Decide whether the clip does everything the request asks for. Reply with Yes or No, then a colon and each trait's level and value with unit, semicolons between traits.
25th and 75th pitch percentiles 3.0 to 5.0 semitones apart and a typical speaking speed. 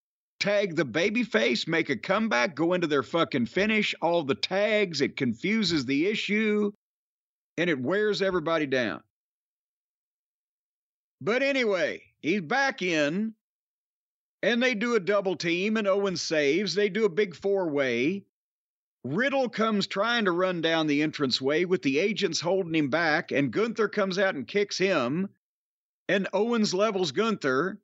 Yes: average, 3.8 semitones; average, 145 wpm